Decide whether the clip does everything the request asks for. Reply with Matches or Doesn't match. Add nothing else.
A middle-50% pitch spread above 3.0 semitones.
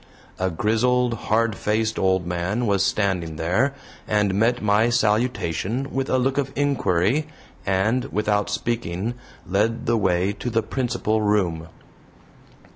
Matches